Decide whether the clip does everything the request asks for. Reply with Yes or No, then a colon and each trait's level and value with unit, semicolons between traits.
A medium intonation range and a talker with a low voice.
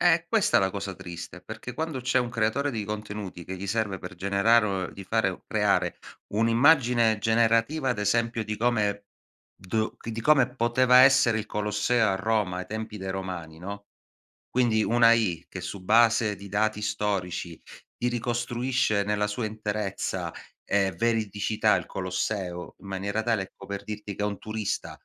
Yes: average, 3.0 semitones; low, 105 Hz